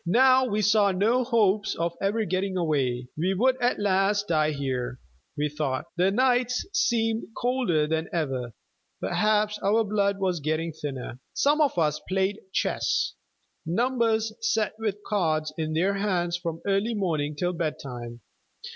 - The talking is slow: No, average, 150 wpm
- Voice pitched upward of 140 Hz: Yes, high, 190 Hz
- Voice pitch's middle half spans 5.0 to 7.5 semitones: Yes, wide, 5.6 semitones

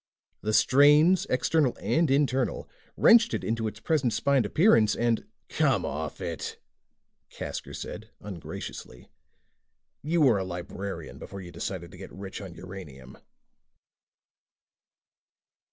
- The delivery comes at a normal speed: No, slow, 120 wpm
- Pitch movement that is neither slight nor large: No, wide, 7.2 semitones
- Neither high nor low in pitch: No, low, 110 Hz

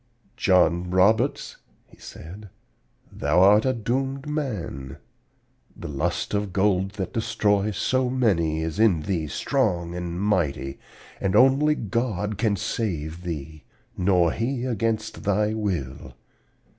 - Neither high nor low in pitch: No, low, 100 Hz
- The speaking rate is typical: No, slow, 120 wpm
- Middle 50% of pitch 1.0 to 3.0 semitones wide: No, average, 4.7 semitones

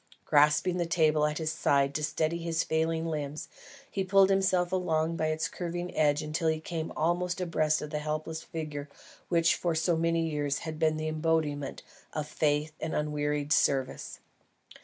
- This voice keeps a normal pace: Yes, average, 170 wpm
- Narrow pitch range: Yes, narrow, 1.7 semitones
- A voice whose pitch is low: No, medium, 155 Hz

